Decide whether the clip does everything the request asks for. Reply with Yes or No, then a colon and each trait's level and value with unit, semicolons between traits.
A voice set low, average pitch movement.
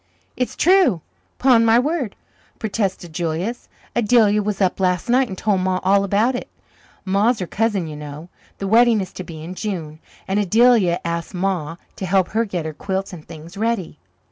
No: high, 195 Hz; average, 4.5 semitones